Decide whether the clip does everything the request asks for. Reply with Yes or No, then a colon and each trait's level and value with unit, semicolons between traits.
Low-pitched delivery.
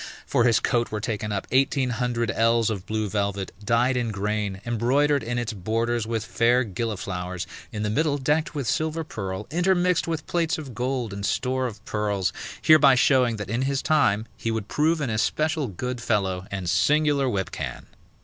Yes: low, 115 Hz